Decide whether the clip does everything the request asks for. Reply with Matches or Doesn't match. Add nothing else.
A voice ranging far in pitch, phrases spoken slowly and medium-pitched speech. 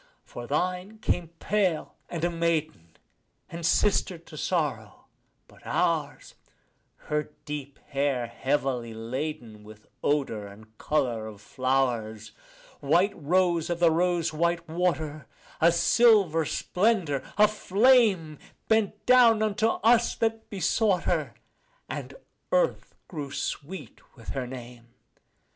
Matches